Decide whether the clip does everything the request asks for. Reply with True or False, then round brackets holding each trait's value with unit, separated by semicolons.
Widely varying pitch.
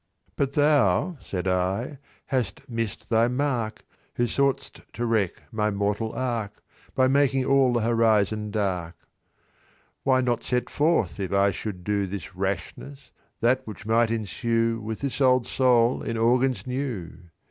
False (4.0 semitones)